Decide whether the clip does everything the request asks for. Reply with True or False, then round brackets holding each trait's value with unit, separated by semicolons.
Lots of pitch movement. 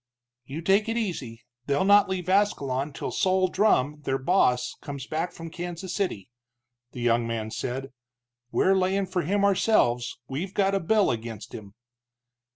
True (7.1 semitones)